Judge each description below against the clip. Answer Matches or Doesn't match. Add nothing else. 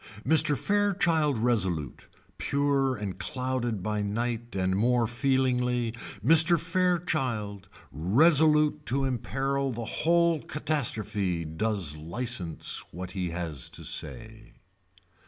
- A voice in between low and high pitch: Doesn't match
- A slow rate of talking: Matches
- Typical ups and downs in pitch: Doesn't match